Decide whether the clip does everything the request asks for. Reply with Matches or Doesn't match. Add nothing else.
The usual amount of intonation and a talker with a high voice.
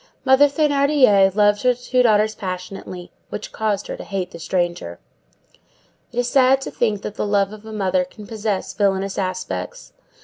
Matches